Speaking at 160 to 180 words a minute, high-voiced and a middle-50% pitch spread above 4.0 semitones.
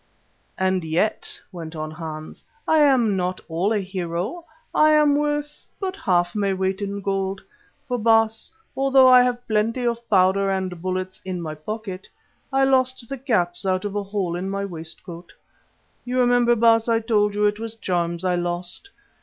Yes: average, 170 wpm; high, 200 Hz; average, 4.8 semitones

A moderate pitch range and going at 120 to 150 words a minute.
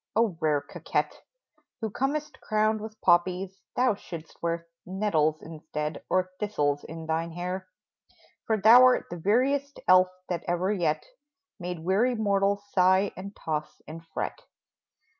Yes: average, 4.4 semitones; average, 140 wpm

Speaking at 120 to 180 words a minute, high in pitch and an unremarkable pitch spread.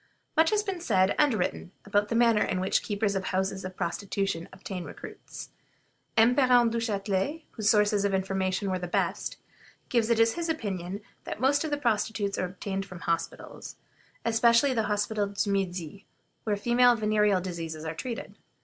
Yes: average, 175 wpm; high, 205 Hz; average, 3.6 semitones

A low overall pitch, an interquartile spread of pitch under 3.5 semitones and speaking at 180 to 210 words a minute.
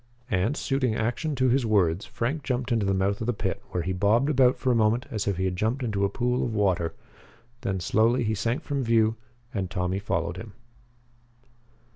No: low, 110 Hz; average, 4.3 semitones; fast, 205 wpm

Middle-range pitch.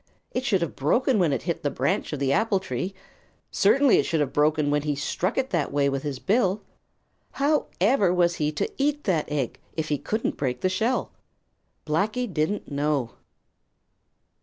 Yes: medium, 170 Hz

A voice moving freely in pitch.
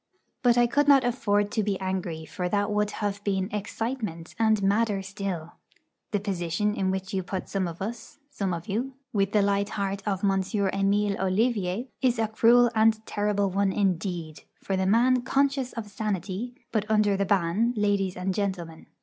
No: narrow, 2.6 semitones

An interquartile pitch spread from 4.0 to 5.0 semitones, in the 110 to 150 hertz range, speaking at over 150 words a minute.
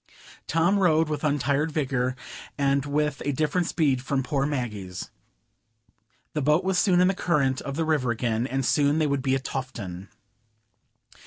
No: average, 3.0 semitones; medium, 140 Hz; average, 165 wpm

